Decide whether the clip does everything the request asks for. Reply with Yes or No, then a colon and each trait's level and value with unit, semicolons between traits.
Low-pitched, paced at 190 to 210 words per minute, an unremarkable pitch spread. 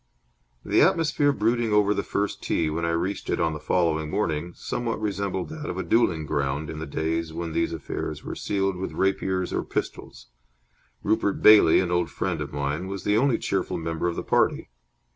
Yes: very low, 90 Hz; average, 195 wpm; average, 4.2 semitones